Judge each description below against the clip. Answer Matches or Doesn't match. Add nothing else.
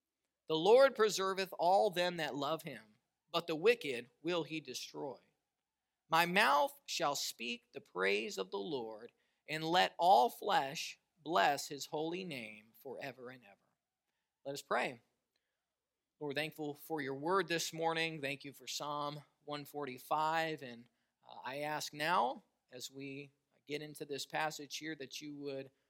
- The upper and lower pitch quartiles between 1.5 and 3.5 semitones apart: Matches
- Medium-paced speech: Matches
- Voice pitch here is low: Doesn't match